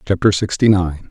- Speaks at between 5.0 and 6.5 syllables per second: Yes, 5.1 syllables/s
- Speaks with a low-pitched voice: Yes, very low, 95 Hz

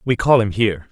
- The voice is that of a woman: No, male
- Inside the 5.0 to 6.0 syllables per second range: No, 6.2 syllables/s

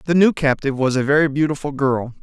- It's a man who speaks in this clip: Yes, male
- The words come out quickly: Yes, fast, 215 wpm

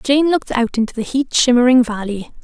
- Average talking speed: Yes, average, 195 wpm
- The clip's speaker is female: Yes, female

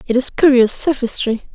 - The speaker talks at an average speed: Yes, average, 155 wpm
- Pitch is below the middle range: No, very high, 250 Hz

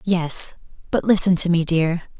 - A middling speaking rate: Yes, average, 165 wpm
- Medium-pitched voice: Yes, medium, 175 Hz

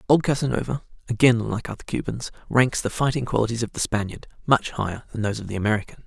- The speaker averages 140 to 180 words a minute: No, average, 200 wpm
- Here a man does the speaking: Yes, male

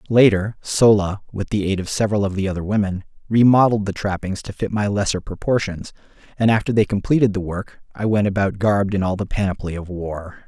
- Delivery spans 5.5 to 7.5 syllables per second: Yes, 5.9 syllables/s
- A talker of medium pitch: No, low, 100 Hz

